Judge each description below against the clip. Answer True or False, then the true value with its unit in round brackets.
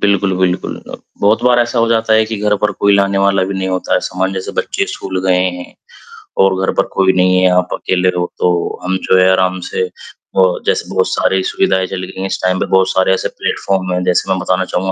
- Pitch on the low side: True (95 Hz)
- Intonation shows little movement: True (1.0 semitones)